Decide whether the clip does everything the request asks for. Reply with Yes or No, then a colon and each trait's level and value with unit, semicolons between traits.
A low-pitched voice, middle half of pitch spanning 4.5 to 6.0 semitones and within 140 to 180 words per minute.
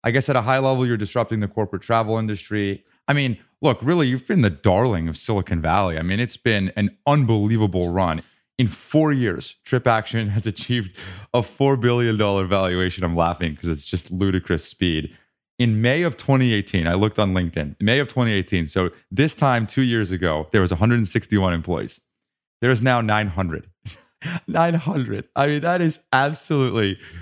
Yes: low, 110 Hz; wide, 5.4 semitones; average, 175 wpm